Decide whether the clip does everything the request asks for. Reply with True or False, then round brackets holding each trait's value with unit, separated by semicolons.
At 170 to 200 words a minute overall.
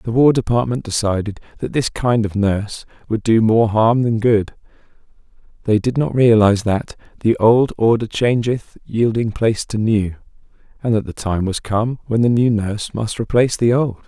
True (180 wpm)